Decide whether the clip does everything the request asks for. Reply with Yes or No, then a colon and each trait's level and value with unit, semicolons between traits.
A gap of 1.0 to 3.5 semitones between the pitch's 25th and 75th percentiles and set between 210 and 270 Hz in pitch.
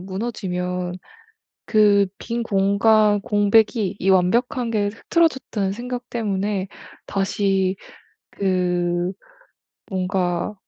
No: average, 2.9 semitones; high, 200 Hz